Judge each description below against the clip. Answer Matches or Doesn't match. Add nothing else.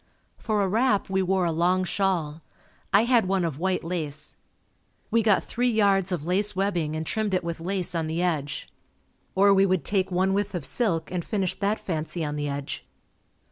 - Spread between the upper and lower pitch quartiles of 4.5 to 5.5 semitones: Doesn't match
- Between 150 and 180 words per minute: Doesn't match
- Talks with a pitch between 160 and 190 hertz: Matches